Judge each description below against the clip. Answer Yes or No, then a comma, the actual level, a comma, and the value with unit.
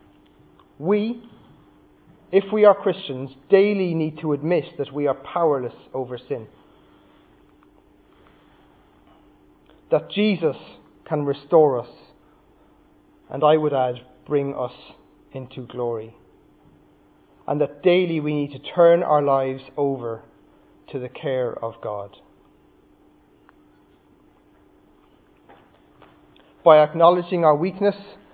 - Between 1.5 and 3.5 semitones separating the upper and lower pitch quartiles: No, average, 5.2 semitones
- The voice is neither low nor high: Yes, medium, 150 Hz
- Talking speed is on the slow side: Yes, slow, 100 wpm